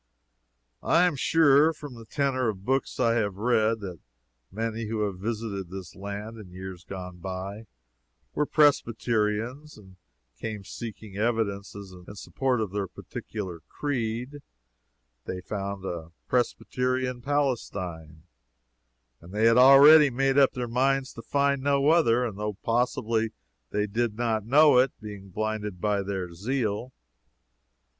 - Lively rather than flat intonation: No, average, 4.5 semitones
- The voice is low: Yes, low, 110 Hz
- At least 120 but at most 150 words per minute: Yes, slow, 135 wpm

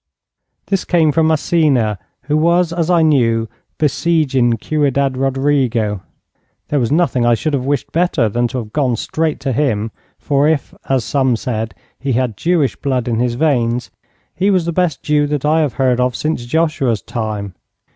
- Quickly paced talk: No, average, 175 wpm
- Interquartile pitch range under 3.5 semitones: No, average, 4.6 semitones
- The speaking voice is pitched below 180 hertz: Yes, low, 135 Hz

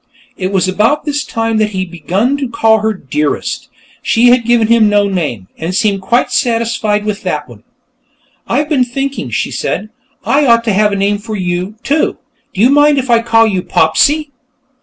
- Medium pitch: No, high, 220 Hz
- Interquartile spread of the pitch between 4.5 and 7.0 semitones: No, average, 3.8 semitones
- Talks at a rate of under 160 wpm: No, average, 195 wpm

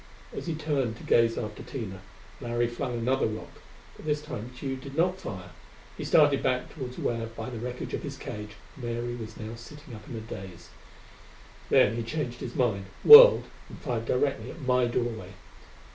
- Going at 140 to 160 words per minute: No, average, 185 wpm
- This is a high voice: No, low, 120 Hz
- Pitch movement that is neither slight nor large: Yes, average, 3.2 semitones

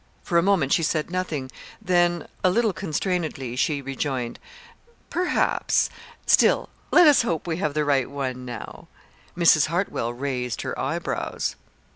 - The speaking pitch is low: No, medium, 155 Hz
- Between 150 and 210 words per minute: No, average, 140 wpm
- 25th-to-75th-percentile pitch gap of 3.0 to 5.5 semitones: Yes, average, 5.1 semitones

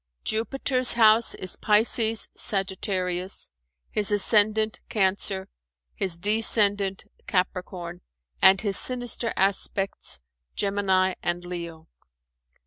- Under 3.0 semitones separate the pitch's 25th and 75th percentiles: Yes, narrow, 2.6 semitones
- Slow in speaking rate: Yes, slow, 85 wpm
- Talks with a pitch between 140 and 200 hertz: Yes, high, 195 Hz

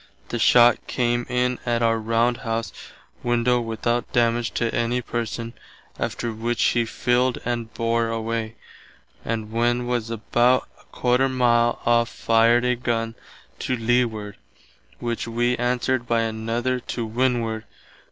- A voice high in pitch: No, low, 120 Hz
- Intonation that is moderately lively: No, narrow, 1.2 semitones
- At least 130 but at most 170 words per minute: Yes, slow, 135 wpm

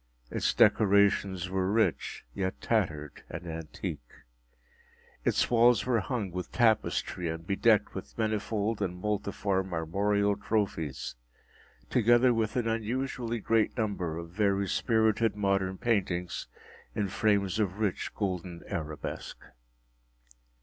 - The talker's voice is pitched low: Yes, low, 100 Hz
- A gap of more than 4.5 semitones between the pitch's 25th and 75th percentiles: No, average, 3.3 semitones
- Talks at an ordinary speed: No, slow, 115 wpm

